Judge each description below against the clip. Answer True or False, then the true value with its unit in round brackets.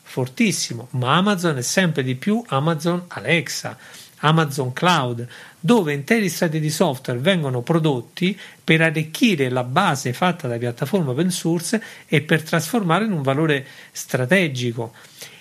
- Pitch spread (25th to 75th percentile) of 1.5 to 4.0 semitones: False (5.3 semitones)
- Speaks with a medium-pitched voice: True (160 Hz)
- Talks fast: False (130 wpm)